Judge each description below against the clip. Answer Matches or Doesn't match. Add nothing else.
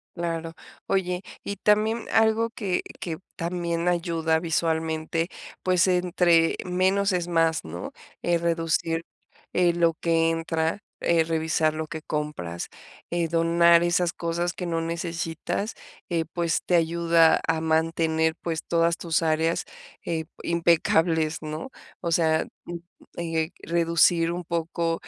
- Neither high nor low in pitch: Matches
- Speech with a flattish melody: Matches